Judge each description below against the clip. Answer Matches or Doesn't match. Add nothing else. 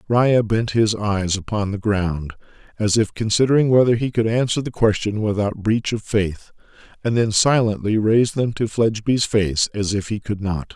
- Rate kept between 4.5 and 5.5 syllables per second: Matches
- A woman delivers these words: Doesn't match